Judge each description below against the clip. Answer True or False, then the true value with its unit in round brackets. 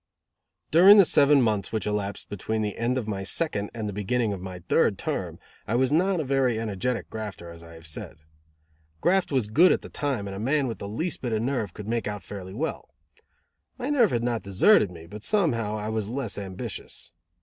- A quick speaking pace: True (215 wpm)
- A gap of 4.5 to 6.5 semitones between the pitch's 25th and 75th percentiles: True (5.2 semitones)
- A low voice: True (110 Hz)